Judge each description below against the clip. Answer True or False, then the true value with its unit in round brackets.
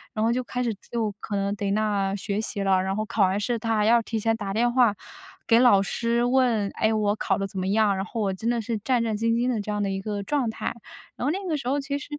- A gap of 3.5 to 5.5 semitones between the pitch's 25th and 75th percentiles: False (2.8 semitones)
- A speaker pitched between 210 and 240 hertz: True (220 Hz)